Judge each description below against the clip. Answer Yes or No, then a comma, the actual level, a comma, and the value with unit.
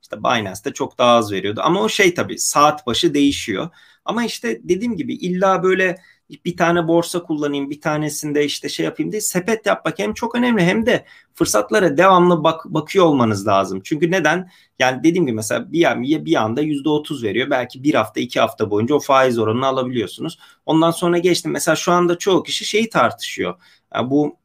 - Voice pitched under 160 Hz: No, medium, 165 Hz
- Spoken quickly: Yes, fast, 190 wpm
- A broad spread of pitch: No, average, 4.5 semitones